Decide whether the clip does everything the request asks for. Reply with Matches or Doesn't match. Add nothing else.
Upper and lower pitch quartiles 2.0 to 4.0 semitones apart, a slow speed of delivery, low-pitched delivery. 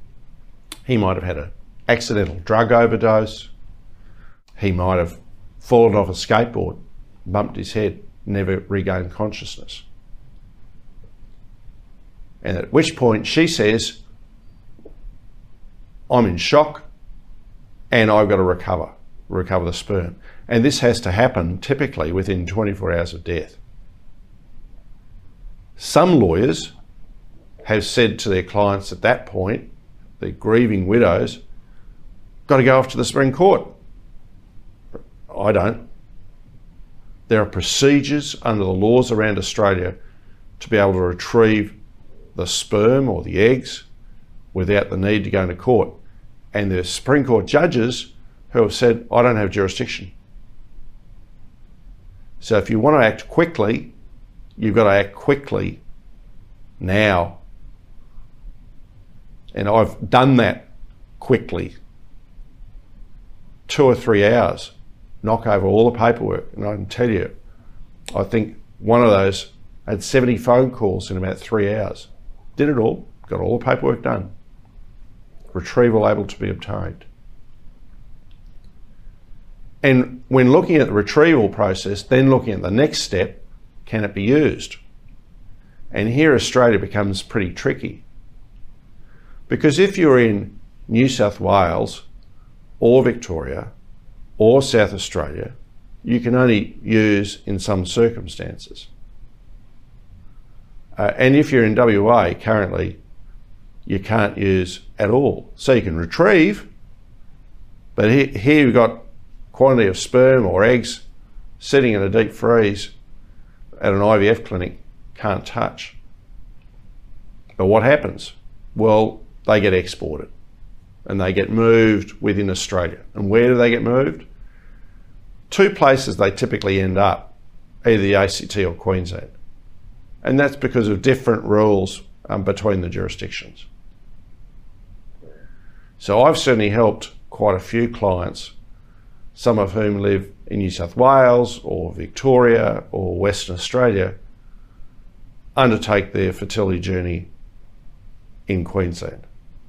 Matches